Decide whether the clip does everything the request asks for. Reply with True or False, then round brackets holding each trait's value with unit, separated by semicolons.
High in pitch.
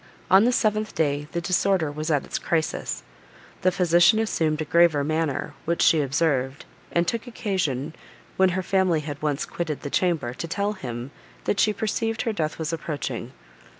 False (165 Hz)